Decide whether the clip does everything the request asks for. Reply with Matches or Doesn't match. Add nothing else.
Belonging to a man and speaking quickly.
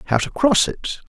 Matches